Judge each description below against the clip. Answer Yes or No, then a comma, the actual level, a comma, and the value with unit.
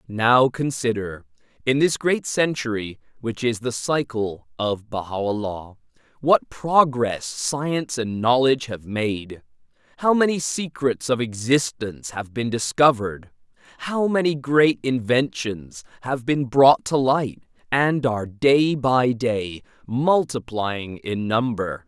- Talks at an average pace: No, slow, 120 wpm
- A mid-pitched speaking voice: No, low, 125 Hz